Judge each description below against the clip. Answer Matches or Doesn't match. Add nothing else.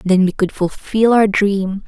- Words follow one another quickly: Doesn't match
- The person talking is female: Matches